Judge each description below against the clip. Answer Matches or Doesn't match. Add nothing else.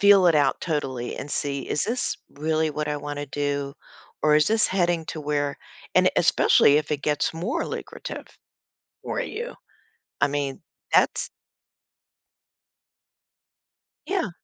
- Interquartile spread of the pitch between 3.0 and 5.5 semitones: Matches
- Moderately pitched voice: Matches